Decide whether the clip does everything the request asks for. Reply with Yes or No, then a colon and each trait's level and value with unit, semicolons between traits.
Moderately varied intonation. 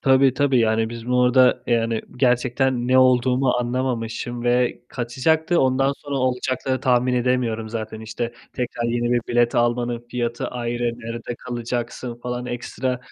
No: narrow, 1.3 semitones